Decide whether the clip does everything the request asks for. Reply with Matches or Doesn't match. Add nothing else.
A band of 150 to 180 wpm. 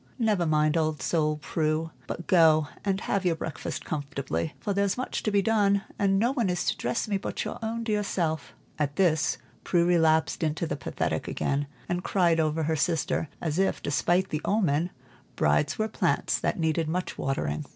Doesn't match